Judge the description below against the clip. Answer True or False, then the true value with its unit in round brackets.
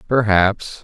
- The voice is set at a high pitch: False (105 Hz)